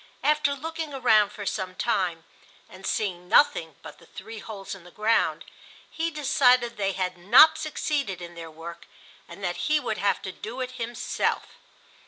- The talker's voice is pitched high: Yes, high, 215 Hz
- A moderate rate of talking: Yes, average, 175 wpm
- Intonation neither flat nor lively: No, wide, 6.5 semitones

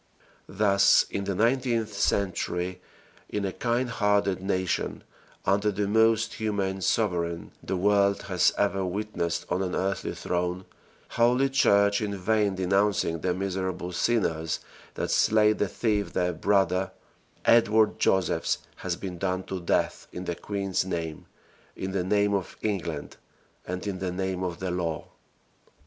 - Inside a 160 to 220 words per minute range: No, average, 140 wpm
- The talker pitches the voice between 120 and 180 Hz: No, very low, 95 Hz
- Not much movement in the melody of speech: Yes, narrow, 2.3 semitones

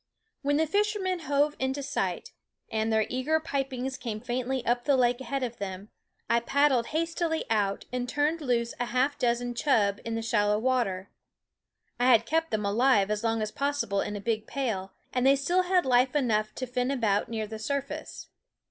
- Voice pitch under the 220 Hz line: No, very high, 250 Hz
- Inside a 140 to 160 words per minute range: No, average, 195 wpm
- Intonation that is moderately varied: Yes, average, 4.2 semitones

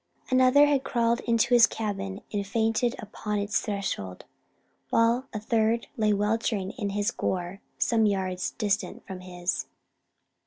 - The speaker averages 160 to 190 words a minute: No, average, 140 wpm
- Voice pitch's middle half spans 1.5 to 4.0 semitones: Yes, average, 2.8 semitones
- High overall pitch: Yes, high, 210 Hz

